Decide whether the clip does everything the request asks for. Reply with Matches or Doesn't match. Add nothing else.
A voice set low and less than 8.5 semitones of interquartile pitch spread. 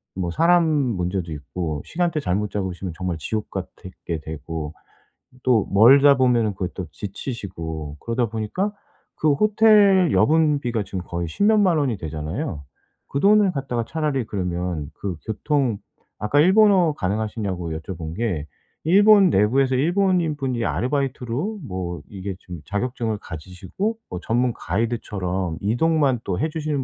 Doesn't match